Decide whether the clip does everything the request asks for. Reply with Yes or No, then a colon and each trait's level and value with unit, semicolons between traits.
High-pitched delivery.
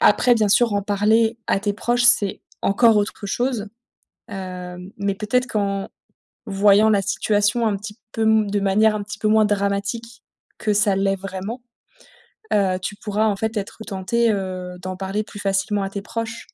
Yes: high, 205 Hz